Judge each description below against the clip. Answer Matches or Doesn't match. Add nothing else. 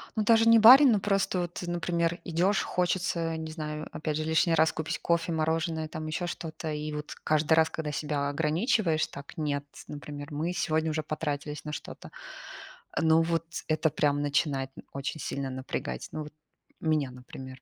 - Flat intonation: Matches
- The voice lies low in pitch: Doesn't match